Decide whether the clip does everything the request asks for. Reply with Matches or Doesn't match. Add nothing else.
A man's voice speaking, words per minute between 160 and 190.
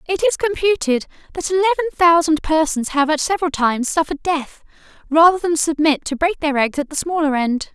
Doesn't match